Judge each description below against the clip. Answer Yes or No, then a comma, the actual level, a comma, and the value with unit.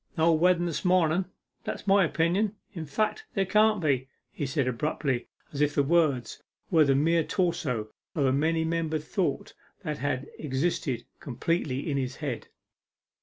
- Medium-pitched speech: Yes, medium, 155 Hz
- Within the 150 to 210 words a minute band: Yes, average, 160 wpm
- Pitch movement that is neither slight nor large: Yes, average, 3.9 semitones